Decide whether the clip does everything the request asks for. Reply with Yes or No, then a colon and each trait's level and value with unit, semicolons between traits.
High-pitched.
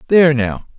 No: medium, 140 Hz